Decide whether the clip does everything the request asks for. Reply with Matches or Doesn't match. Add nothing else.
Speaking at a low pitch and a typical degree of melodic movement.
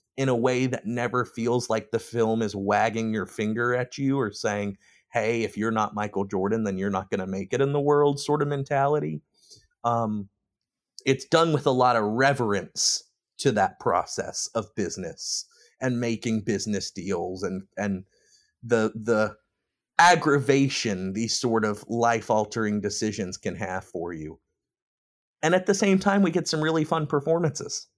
Matches